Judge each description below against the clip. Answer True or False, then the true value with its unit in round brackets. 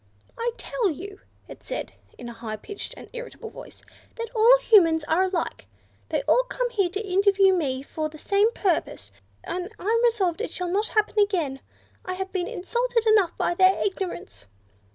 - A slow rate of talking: False (175 wpm)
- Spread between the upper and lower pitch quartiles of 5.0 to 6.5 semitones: False (4.3 semitones)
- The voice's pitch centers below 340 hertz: False (385 Hz)